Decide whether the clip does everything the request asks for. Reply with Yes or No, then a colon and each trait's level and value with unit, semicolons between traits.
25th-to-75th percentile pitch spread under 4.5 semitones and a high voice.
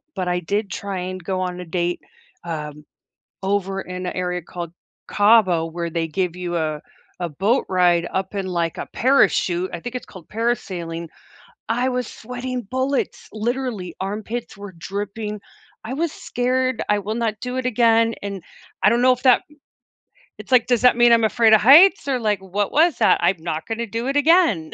No: average, 5.3 semitones; high, 205 Hz